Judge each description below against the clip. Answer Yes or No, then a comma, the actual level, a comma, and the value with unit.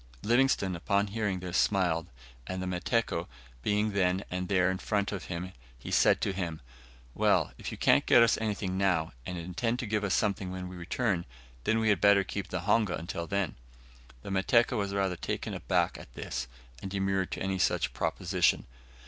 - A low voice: Yes, very low, 95 Hz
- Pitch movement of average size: No, narrow, 2.2 semitones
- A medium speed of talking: Yes, average, 180 wpm